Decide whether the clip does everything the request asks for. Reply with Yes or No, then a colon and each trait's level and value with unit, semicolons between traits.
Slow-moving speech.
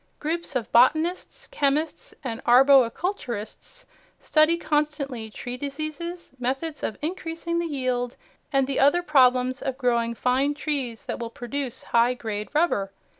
Yes: slow, 130 wpm